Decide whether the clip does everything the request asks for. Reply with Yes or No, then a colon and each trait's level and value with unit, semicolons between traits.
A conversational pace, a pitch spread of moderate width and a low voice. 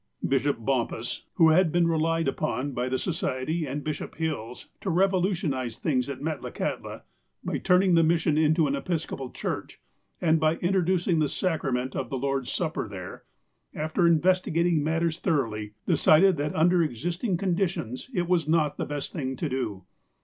No: average, 160 wpm; average, 4.2 semitones; medium, 155 Hz